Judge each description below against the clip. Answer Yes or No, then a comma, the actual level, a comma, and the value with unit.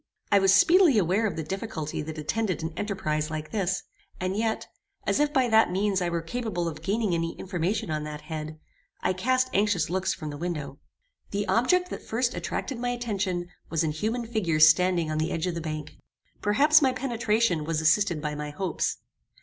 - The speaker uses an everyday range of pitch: No, wide, 5.8 semitones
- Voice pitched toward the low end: No, medium, 185 Hz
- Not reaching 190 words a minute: No, average, 195 wpm